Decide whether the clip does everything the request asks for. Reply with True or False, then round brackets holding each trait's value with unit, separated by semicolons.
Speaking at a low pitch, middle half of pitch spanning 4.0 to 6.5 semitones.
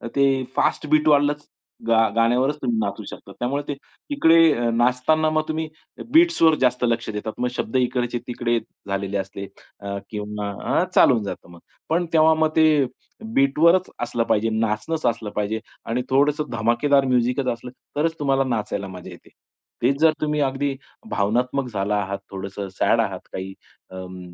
True (125 Hz; 5.6 semitones)